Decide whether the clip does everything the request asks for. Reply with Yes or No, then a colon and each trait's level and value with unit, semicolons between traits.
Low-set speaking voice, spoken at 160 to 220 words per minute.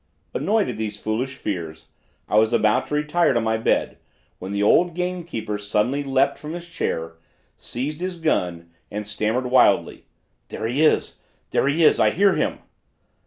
Yes: low, 125 Hz; average, 165 wpm